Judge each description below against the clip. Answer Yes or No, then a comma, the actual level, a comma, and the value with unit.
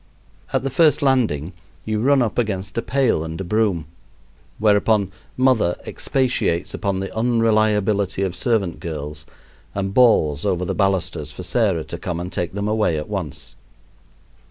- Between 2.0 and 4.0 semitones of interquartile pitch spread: No, average, 4.5 semitones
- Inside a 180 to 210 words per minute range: No, average, 155 wpm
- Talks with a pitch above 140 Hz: No, low, 100 Hz